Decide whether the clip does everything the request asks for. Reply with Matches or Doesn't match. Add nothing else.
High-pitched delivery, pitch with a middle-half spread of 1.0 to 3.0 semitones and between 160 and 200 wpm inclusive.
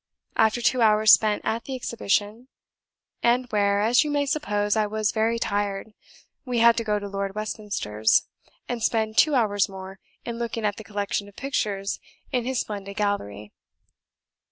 Matches